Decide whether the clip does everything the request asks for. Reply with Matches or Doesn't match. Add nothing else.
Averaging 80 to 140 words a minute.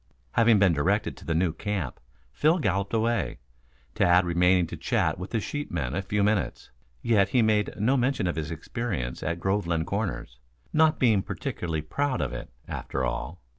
Doesn't match